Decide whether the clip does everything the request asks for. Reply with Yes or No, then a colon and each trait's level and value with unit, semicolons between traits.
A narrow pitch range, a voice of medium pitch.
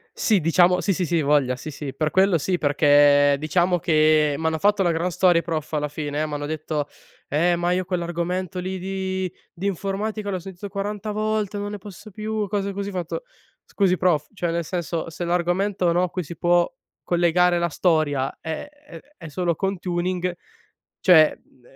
No: average, 3.3 semitones; medium, 175 Hz